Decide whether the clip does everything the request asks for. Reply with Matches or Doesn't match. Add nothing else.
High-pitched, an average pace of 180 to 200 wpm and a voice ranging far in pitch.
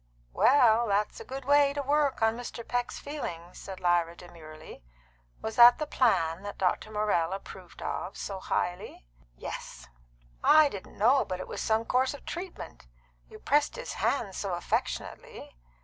Doesn't match